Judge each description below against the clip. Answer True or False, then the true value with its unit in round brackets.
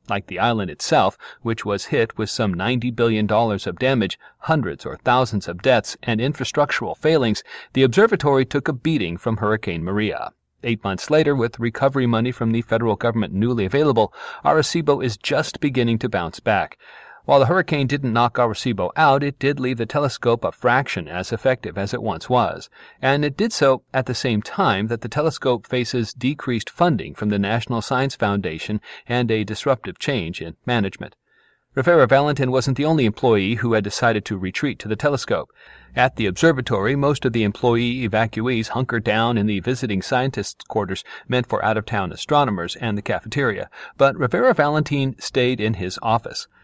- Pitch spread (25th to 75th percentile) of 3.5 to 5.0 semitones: True (3.8 semitones)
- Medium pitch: False (120 Hz)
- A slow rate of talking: False (180 wpm)